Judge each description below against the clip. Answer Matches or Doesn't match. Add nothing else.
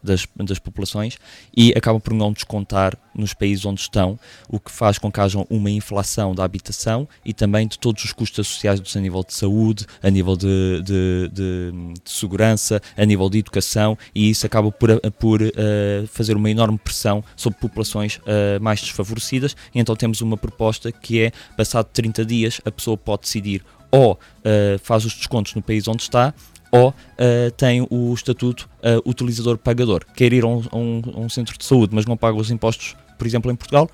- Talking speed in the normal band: Matches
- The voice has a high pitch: Doesn't match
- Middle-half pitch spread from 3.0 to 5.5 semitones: Doesn't match